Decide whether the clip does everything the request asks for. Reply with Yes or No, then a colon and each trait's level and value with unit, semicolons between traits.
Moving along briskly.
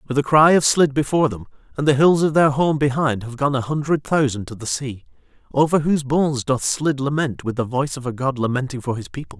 Yes: fast, 245 wpm